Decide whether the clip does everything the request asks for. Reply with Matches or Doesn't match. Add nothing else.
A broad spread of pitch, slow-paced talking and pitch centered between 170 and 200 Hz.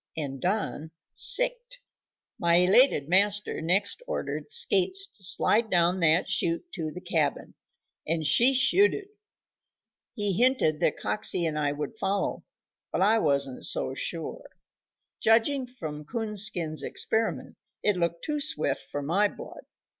Matches